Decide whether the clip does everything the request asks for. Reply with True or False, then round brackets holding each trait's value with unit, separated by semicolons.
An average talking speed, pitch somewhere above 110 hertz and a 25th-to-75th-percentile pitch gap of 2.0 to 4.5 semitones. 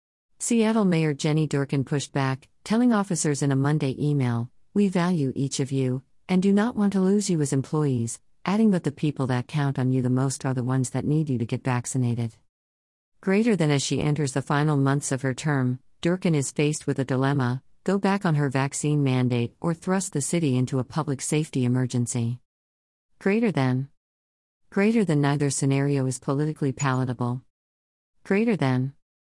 True (180 wpm; 140 Hz; 3.5 semitones)